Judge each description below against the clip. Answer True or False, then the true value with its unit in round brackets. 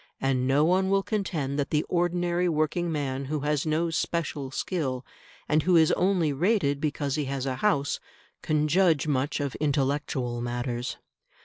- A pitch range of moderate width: True (4.0 semitones)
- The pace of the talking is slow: False (165 wpm)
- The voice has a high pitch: False (150 Hz)